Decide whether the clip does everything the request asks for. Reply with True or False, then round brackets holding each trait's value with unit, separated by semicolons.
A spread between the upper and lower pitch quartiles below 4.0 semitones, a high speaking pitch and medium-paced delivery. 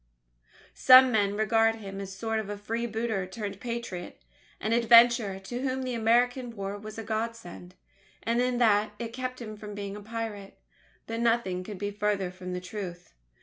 True (2.8 semitones; 220 Hz; 175 wpm)